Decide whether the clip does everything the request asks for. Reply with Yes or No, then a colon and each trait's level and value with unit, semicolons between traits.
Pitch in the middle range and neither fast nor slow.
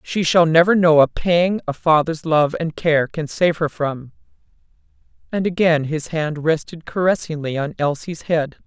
Yes: medium, 160 Hz; average, 165 wpm